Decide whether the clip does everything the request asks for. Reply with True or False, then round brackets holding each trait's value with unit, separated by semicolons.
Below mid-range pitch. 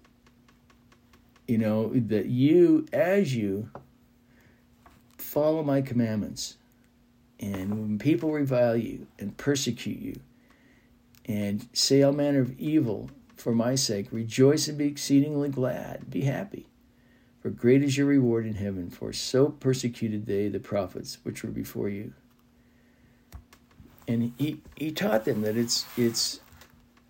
True (120 Hz)